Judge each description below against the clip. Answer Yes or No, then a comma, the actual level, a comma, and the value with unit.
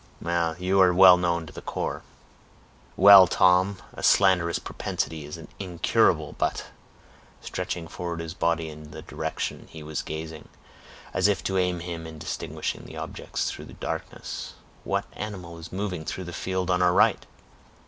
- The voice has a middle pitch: No, very low, 90 Hz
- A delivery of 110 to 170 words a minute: Yes, average, 150 wpm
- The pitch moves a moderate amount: No, narrow, 2.3 semitones